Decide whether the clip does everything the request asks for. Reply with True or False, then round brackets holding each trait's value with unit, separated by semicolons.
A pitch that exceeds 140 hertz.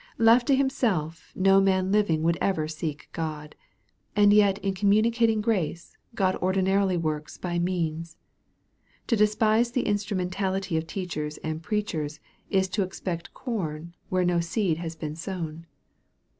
True (185 Hz)